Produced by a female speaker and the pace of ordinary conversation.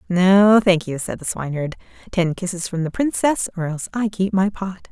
No: female; fast, 210 wpm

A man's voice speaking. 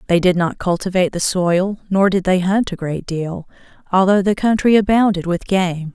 No: female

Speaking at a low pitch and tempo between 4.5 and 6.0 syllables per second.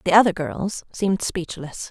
No: medium, 185 Hz; 4.6 syllables/s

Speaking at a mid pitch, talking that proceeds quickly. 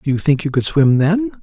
Yes: medium, 155 Hz; fast, 295 wpm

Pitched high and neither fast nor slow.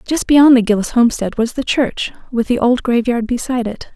No: high, 240 Hz; fast, 210 wpm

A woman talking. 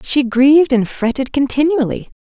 Yes: female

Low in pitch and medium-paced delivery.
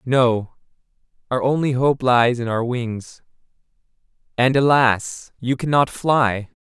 No: low, 125 Hz; slow, 110 wpm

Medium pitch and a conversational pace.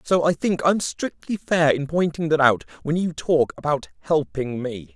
Yes: medium, 150 Hz; average, 195 wpm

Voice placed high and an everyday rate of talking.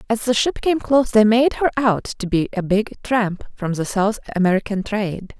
No: high, 215 Hz; fast, 210 wpm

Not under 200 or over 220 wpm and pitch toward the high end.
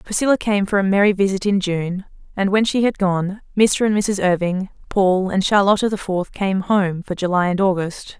Yes: fast, 205 wpm; high, 195 Hz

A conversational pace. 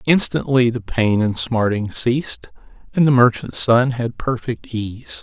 Yes: average, 150 wpm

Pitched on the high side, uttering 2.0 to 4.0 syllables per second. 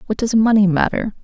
No: high, 210 Hz; 5.9 syllables/s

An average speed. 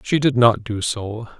No: fast, 215 wpm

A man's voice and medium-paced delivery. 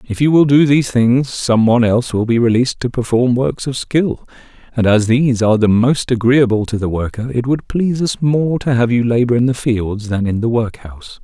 No: male; fast, 230 wpm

